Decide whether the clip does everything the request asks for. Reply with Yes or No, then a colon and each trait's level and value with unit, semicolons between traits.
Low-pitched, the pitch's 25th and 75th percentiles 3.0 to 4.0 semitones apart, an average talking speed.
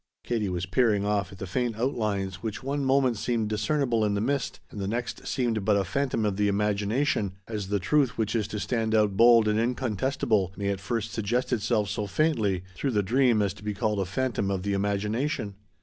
No: low, 105 Hz; average, 3.3 semitones; fast, 210 wpm